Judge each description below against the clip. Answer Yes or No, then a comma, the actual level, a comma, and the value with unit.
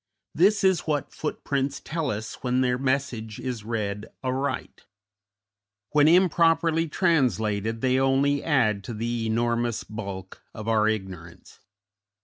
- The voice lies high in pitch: No, low, 125 Hz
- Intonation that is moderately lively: Yes, average, 4.9 semitones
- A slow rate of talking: Yes, slow, 125 wpm